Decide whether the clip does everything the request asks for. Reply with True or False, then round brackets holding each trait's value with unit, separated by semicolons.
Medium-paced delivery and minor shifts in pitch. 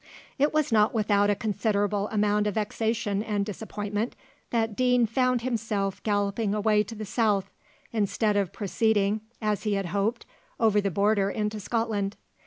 True (155 wpm; 1.7 semitones)